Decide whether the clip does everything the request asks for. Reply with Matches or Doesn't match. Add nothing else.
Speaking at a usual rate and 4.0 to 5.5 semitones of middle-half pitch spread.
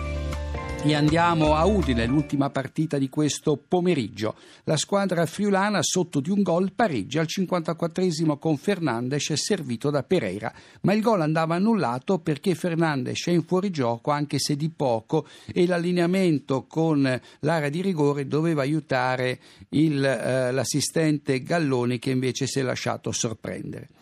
Matches